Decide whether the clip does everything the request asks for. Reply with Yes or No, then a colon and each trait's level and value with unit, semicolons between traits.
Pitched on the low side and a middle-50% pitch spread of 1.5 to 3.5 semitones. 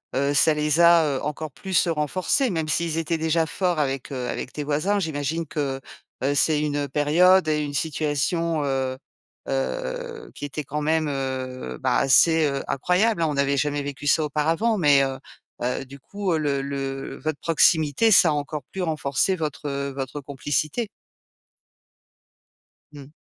No: medium, 150 Hz; average, 3.0 semitones